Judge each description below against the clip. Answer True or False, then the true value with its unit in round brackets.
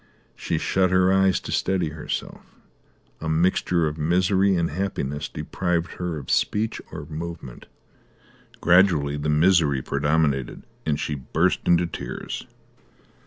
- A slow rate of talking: True (125 wpm)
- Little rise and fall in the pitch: False (3.6 semitones)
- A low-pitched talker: True (85 Hz)